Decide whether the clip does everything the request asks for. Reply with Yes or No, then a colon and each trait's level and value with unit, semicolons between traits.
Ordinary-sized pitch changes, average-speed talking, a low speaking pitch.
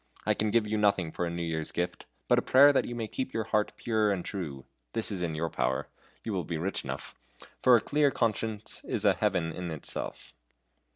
No: average, 4.6 semitones; fast, 225 wpm; low, 105 Hz